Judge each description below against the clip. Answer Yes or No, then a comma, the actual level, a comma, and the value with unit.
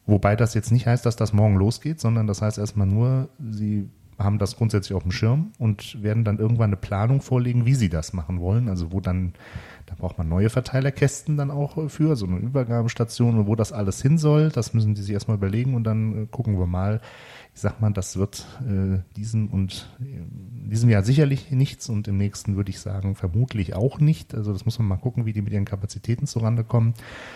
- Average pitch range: Yes, average, 3.3 semitones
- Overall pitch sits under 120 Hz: Yes, low, 110 Hz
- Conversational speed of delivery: No, fast, 220 wpm